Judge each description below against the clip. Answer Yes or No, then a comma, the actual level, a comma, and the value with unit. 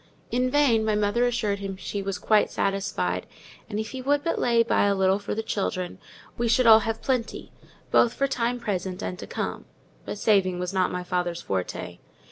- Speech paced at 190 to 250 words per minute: Yes, average, 200 wpm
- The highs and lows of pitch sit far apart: No, average, 3.8 semitones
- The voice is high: Yes, high, 210 Hz